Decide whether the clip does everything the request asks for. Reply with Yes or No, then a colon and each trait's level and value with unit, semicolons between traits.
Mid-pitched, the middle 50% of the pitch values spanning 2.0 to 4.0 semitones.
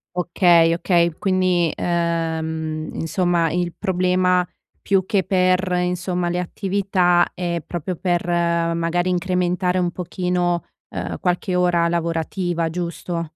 No: medium, 175 Hz; narrow, 1.3 semitones